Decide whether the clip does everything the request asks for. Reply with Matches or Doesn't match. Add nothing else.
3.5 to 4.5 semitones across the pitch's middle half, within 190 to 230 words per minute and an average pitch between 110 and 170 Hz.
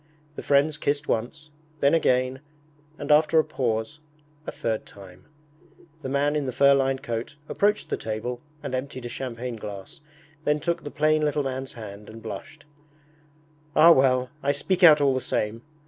Doesn't match